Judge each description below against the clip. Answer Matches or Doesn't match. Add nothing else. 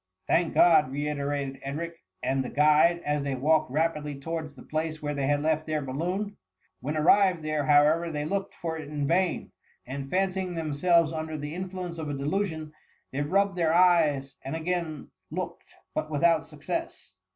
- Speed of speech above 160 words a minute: Matches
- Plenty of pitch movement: Doesn't match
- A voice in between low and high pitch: Matches